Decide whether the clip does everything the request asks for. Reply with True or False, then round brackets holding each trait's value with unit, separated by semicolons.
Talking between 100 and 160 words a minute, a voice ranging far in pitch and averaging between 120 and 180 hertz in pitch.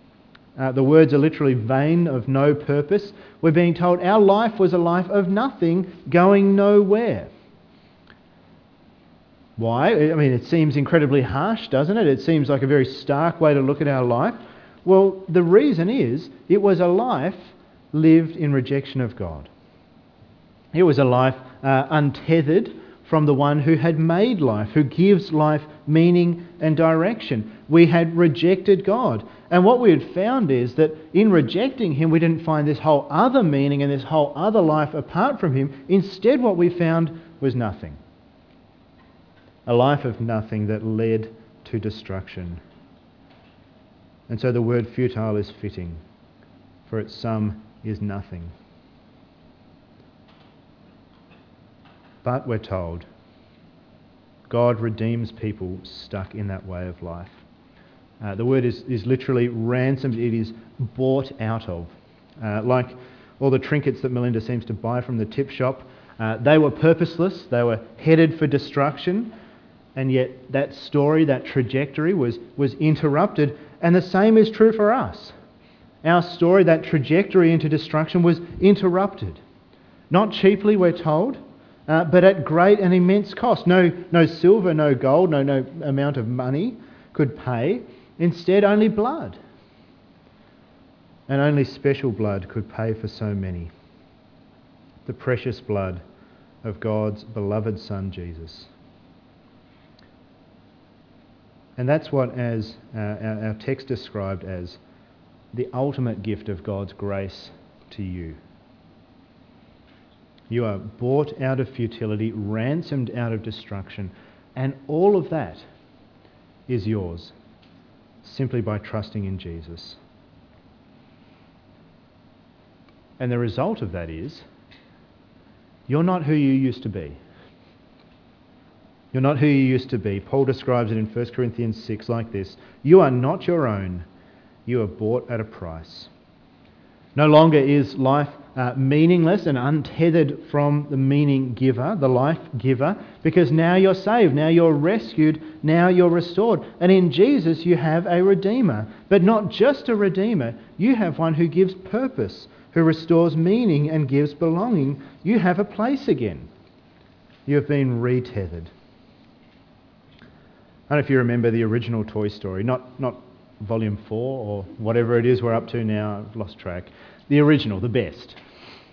True (145 wpm; 6.9 semitones; 135 Hz)